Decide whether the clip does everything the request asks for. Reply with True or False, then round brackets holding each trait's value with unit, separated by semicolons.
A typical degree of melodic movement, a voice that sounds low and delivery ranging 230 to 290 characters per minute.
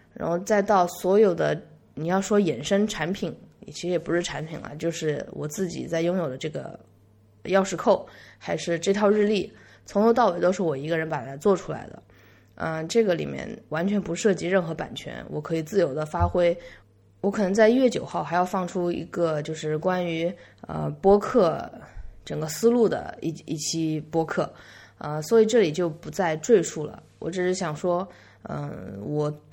False (4.2 semitones; 170 Hz; 265 characters per minute)